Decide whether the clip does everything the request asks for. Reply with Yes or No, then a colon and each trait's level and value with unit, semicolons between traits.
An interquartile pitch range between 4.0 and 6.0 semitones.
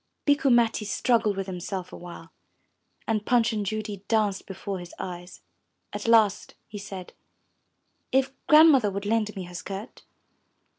No: average, 3.2 semitones